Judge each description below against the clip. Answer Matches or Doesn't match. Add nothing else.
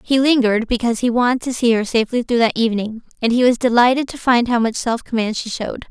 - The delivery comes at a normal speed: Doesn't match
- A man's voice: Doesn't match